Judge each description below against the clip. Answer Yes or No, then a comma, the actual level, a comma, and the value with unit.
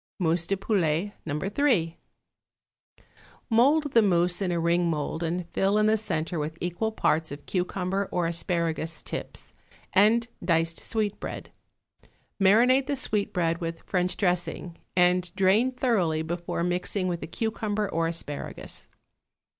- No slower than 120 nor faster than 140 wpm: Yes, slow, 135 wpm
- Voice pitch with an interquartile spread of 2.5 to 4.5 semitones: Yes, average, 3.9 semitones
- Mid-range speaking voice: Yes, medium, 180 Hz